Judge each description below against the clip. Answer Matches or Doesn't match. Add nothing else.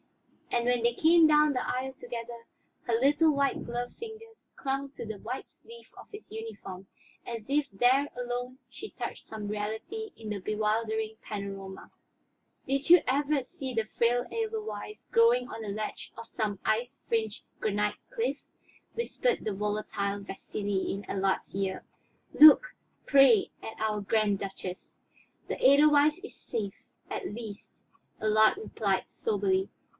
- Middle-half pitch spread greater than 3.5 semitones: Matches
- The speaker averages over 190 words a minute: Doesn't match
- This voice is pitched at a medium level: Doesn't match